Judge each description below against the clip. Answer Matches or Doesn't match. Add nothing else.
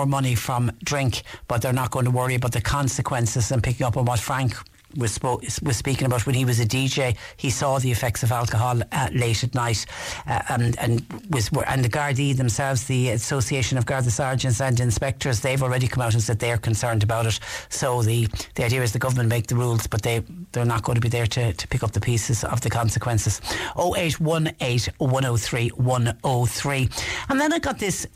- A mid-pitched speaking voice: Doesn't match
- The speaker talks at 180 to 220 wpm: Matches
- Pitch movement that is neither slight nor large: Doesn't match